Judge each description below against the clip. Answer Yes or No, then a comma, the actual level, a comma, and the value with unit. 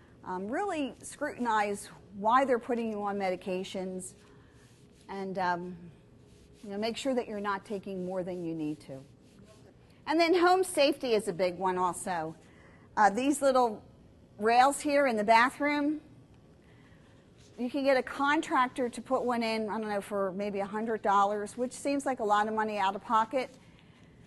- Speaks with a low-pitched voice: No, high, 220 Hz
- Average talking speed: Yes, average, 170 wpm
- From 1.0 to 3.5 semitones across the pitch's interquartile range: No, average, 5.1 semitones